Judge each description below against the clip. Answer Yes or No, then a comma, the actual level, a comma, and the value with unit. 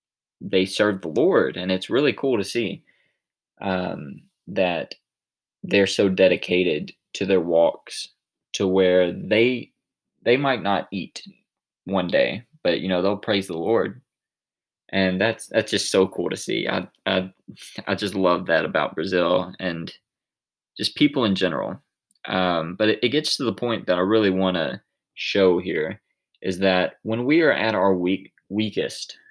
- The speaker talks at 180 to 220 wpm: No, average, 160 wpm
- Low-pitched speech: Yes, very low, 95 Hz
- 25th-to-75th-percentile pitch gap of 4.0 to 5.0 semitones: No, average, 2.7 semitones